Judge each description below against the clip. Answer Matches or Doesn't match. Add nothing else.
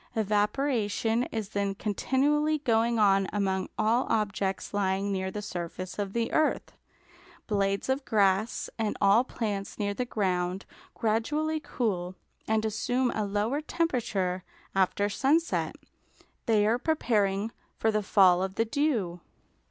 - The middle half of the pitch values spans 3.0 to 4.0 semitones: Matches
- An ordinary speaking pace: Doesn't match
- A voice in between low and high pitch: Doesn't match